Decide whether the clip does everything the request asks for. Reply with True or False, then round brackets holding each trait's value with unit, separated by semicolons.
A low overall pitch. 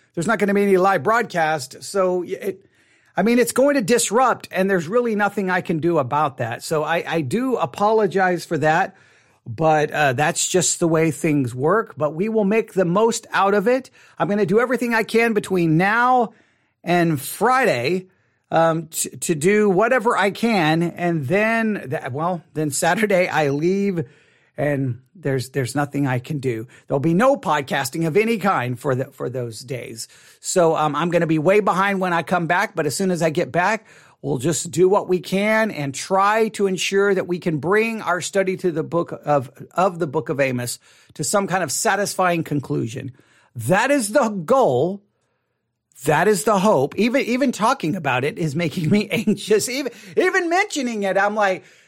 False (180 Hz)